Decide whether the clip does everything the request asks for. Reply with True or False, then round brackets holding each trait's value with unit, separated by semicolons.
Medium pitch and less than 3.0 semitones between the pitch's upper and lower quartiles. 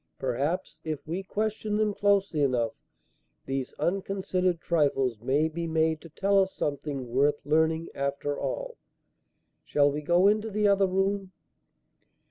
False (165 Hz; 5.3 semitones)